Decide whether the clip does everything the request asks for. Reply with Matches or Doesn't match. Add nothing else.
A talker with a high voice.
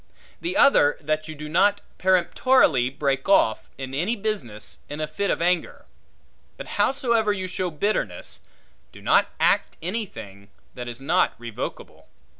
Doesn't match